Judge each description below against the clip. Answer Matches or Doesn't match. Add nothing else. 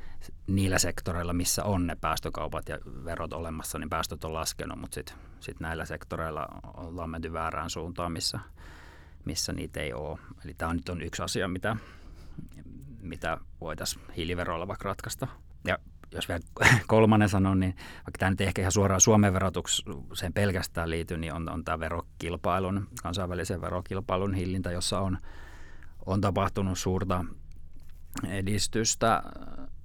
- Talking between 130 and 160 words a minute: Matches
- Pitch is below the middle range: Matches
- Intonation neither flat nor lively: Matches